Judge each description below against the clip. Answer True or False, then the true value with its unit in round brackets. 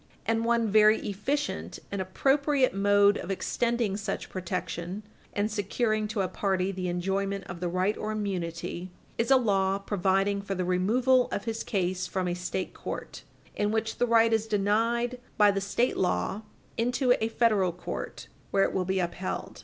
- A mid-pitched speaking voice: False (200 Hz)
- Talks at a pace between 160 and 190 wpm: True (170 wpm)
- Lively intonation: False (3.3 semitones)